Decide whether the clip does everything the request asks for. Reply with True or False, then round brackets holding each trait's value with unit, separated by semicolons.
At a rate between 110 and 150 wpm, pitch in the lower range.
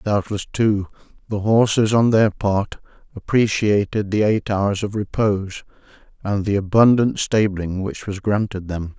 True (140 wpm; 100 Hz)